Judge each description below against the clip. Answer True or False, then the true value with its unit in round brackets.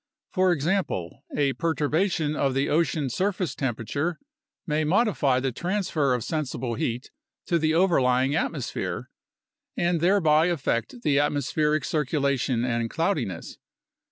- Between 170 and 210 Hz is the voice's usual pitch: False (150 Hz)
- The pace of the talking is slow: True (120 wpm)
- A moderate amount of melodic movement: True (4.5 semitones)